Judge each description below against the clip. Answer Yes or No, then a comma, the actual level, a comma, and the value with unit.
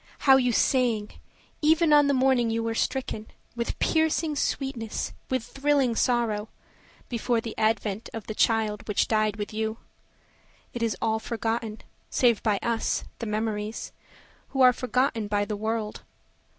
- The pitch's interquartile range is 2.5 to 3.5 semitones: Yes, average, 3.0 semitones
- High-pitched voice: Yes, high, 230 Hz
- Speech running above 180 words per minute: No, average, 150 wpm